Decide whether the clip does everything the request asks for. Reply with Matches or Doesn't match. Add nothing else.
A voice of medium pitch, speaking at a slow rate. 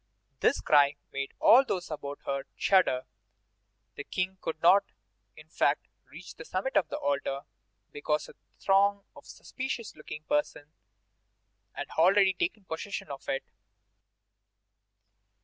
Matches